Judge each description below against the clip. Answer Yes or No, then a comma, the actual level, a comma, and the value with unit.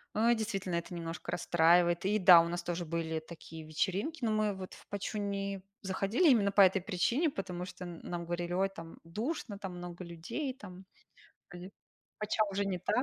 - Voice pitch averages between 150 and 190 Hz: Yes, medium, 185 Hz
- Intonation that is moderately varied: Yes, average, 3.0 semitones